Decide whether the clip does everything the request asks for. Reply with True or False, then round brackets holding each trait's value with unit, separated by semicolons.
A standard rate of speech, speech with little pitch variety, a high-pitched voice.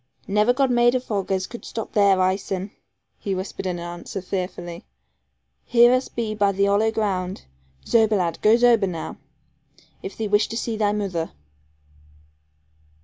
False (150 wpm; 3.1 semitones; 205 Hz)